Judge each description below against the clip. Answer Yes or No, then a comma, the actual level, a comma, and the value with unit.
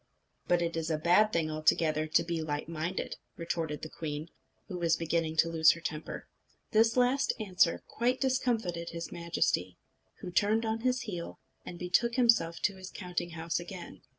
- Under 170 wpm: No, average, 175 wpm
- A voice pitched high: No, medium, 170 Hz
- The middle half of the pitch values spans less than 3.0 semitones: No, average, 4.7 semitones